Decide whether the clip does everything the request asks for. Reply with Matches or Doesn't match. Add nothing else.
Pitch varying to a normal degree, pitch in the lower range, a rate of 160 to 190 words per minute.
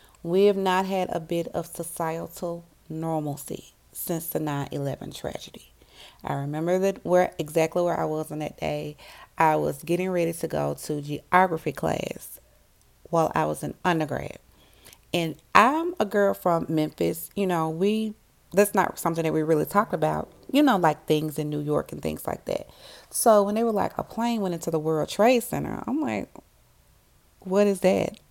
Doesn't match